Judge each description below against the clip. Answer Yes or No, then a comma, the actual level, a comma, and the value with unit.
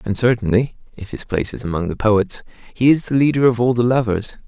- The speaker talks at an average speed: No, fast, 230 wpm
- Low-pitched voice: Yes, low, 115 Hz